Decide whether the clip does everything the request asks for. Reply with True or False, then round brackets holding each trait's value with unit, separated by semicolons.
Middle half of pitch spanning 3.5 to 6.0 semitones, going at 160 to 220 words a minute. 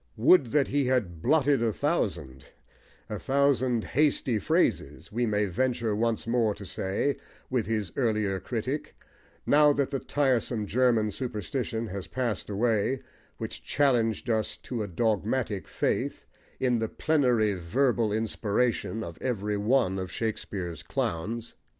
False (3.9 semitones; 135 wpm)